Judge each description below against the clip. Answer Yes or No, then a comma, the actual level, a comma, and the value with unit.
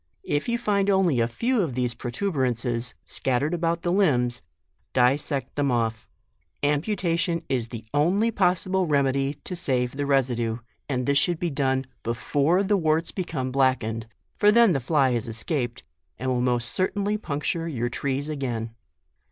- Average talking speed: Yes, average, 170 wpm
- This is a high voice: No, medium, 140 Hz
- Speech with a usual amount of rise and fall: No, wide, 5.9 semitones